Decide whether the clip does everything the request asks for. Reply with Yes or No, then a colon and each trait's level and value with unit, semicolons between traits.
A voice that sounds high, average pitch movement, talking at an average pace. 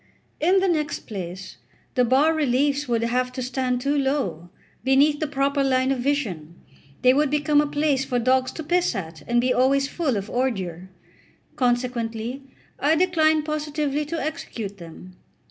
Yes: very high, 265 Hz; average, 3.7 semitones; average, 165 wpm